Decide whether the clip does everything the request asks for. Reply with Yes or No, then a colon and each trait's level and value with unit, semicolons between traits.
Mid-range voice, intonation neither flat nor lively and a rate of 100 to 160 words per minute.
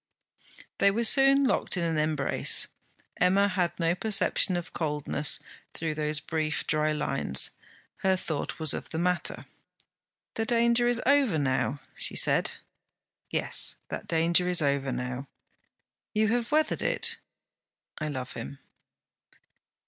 No: medium, 165 Hz; wide, 6.0 semitones; slow, 135 wpm